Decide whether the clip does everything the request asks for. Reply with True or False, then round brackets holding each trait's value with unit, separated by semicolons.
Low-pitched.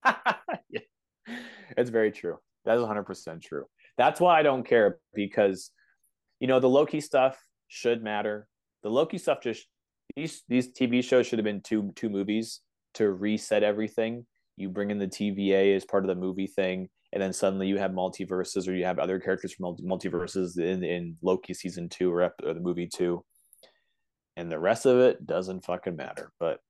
True (100 Hz)